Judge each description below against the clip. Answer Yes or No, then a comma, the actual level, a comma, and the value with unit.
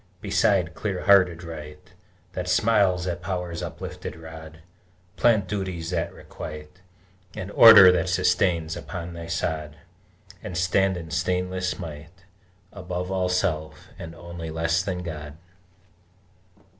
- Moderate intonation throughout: No, narrow, 2.1 semitones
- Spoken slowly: Yes, slow, 120 wpm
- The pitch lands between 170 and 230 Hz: No, very low, 90 Hz